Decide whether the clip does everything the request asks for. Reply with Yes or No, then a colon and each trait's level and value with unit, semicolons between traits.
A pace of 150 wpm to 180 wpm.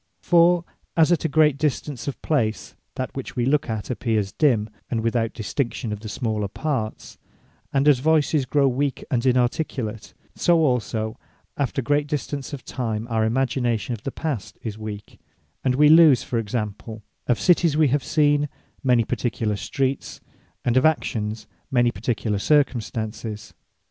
Yes: average, 155 wpm